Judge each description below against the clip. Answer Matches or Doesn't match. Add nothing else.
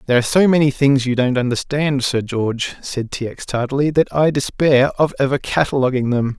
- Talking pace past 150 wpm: Matches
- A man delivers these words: Matches